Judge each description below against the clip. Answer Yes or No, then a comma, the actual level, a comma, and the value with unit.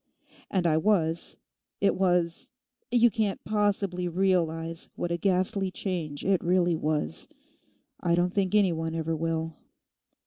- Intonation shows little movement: No, average, 3.1 semitones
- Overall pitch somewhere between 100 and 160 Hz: No, medium, 180 Hz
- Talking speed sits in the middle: No, slow, 125 wpm